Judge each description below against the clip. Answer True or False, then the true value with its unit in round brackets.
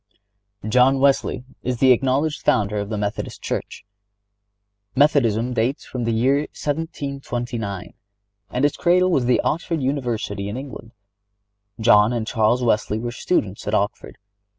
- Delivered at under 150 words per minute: True (140 wpm)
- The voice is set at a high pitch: False (125 Hz)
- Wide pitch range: False (4.2 semitones)